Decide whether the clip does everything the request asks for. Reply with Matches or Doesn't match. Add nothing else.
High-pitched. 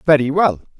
Doesn't match